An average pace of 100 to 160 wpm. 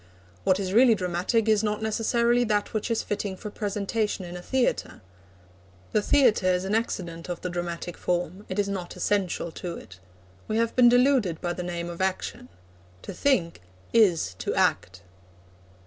No: average, 170 wpm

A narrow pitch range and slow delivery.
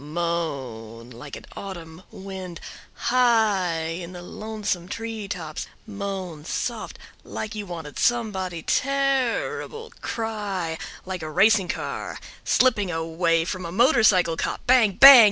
No: average, 4.9 semitones; slow, 120 wpm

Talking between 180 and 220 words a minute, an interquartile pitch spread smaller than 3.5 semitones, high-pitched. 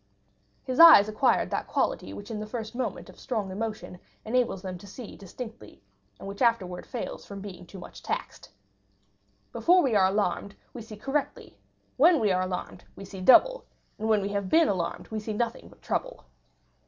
No: average, 185 wpm; average, 3.9 semitones; high, 215 Hz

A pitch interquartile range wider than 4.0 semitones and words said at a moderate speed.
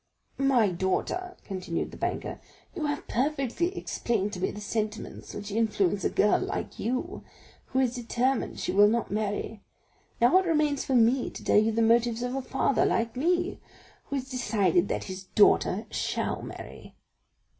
Yes: average, 4.7 semitones; average, 165 wpm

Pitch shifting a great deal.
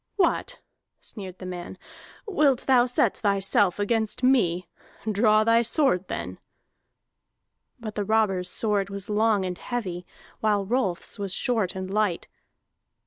No: average, 3.6 semitones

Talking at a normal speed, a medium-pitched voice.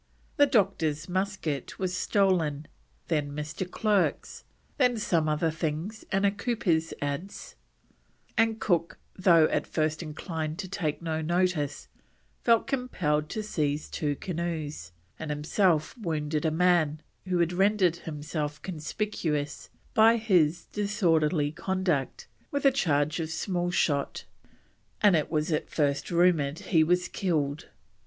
No: slow, 130 wpm; medium, 165 Hz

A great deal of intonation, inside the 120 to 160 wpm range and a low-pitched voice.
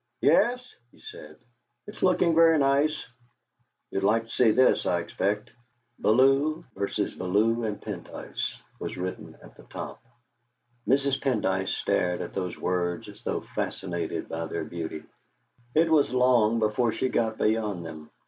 Yes: wide, 6.9 semitones; average, 145 wpm; low, 110 Hz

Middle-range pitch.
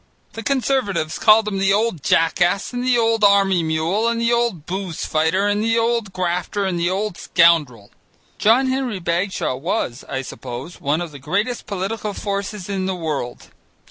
No: high, 195 Hz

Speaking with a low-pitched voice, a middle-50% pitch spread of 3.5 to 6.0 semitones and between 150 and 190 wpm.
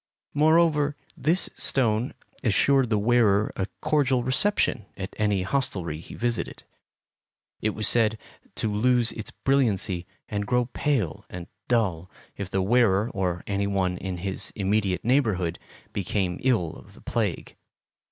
No: low, 105 Hz; average, 4.7 semitones; slow, 135 wpm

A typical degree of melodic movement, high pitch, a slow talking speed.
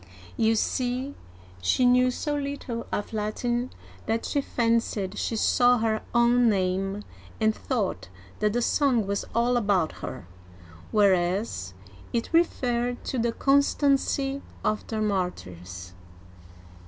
Yes: average, 3.7 semitones; high, 230 Hz; slow, 120 wpm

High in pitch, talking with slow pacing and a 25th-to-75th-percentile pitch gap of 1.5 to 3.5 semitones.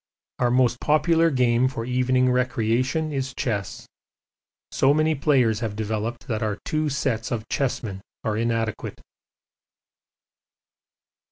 No: low, 125 Hz; slow, 115 wpm; average, 3.1 semitones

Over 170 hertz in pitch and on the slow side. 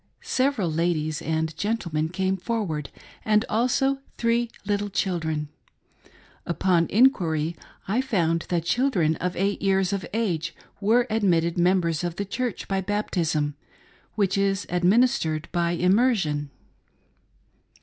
Yes: medium, 185 Hz; slow, 120 wpm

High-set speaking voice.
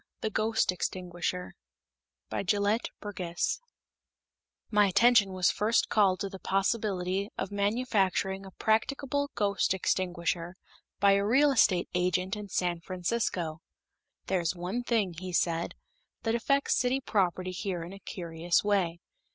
Yes: high, 195 Hz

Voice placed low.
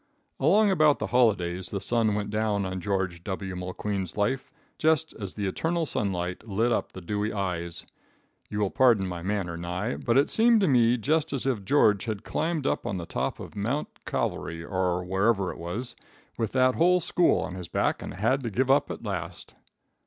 Yes: low, 105 Hz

